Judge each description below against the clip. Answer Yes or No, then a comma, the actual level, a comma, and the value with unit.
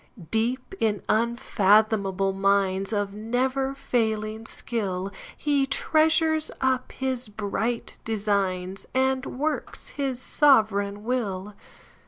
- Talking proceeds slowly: Yes, slow, 80 wpm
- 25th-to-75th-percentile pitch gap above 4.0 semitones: Yes, average, 4.5 semitones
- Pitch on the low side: No, high, 220 Hz